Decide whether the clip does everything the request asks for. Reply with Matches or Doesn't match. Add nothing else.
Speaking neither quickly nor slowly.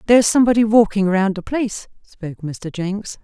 Matches